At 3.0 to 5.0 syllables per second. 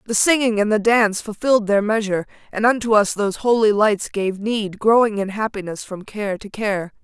No: 5.3 syllables/s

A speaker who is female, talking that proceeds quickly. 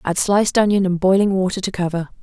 Yes: female; fast, 215 wpm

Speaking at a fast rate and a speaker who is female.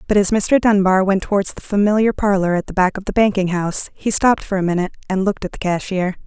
Yes: fast, 250 wpm; female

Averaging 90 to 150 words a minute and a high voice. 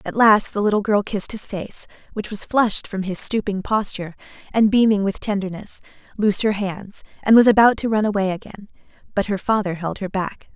No: average, 200 wpm; high, 205 Hz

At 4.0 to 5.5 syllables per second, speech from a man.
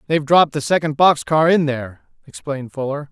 No: 6.2 syllables/s; male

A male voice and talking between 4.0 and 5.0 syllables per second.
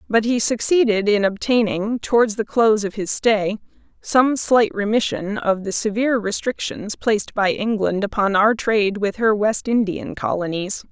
No: female; 4.7 syllables/s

